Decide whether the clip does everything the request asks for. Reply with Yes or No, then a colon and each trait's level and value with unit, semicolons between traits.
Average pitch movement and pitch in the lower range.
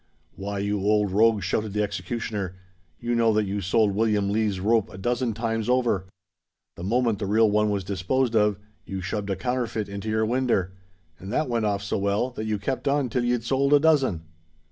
Yes: average, 3.0 semitones; low, 105 Hz